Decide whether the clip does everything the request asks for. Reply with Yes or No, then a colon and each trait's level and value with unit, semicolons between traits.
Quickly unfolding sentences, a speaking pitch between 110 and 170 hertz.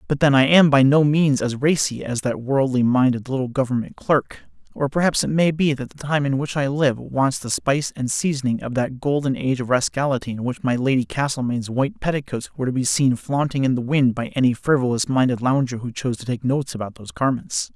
Yes: fast, 225 wpm; low, 135 Hz